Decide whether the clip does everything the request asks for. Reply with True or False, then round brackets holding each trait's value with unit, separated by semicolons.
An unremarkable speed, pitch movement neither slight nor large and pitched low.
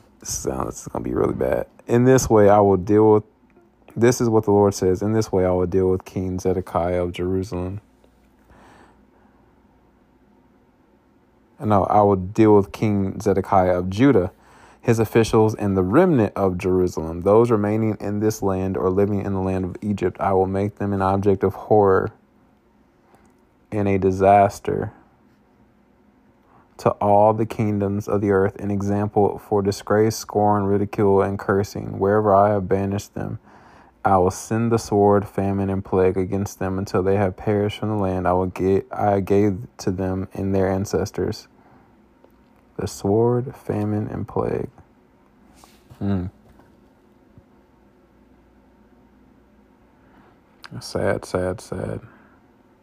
False (145 wpm; 1.9 semitones; 100 Hz)